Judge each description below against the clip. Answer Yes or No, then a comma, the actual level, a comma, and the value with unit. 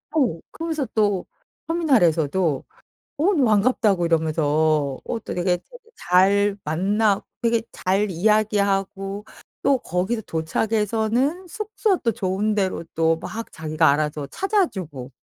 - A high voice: Yes, high, 200 Hz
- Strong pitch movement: Yes, wide, 5.8 semitones